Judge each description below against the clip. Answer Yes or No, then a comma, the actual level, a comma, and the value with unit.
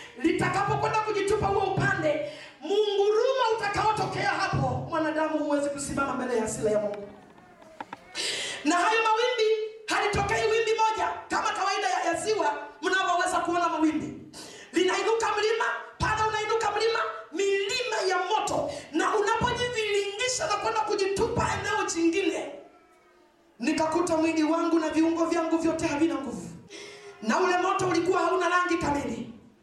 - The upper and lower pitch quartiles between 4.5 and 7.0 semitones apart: Yes, average, 5.0 semitones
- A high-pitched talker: Yes, very high, 360 Hz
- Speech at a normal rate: No, slow, 105 wpm